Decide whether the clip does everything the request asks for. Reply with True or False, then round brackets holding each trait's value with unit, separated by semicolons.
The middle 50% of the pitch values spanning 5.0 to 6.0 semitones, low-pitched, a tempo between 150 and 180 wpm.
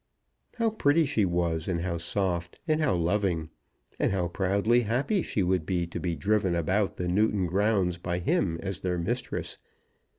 False (3.6 semitones; 95 Hz; 170 wpm)